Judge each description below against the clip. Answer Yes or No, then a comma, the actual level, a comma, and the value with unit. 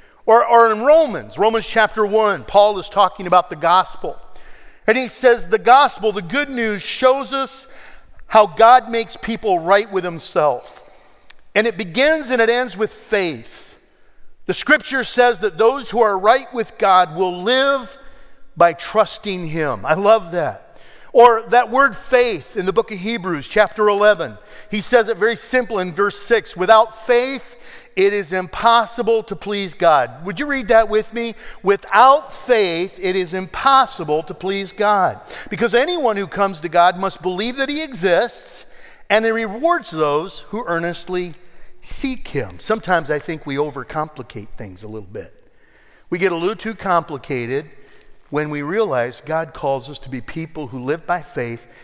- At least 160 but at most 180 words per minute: Yes, average, 165 wpm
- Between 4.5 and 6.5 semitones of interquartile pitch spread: Yes, average, 5.2 semitones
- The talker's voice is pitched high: Yes, high, 210 Hz